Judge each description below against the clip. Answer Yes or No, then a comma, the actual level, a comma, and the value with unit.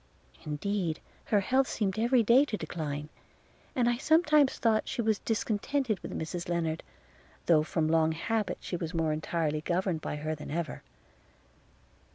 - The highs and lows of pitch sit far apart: Yes, wide, 6.2 semitones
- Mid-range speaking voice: Yes, medium, 180 Hz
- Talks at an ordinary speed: Yes, average, 155 wpm